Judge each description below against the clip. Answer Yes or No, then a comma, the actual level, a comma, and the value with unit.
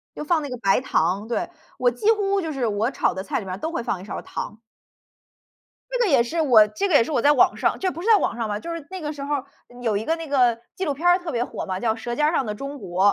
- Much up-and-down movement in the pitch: Yes, wide, 6.6 semitones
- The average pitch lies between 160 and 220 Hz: No, very high, 265 Hz